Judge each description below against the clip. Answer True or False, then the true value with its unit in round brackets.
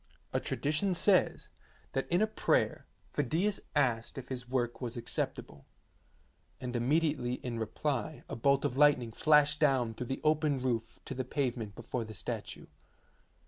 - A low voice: True (130 Hz)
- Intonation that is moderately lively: True (3.8 semitones)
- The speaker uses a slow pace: False (150 wpm)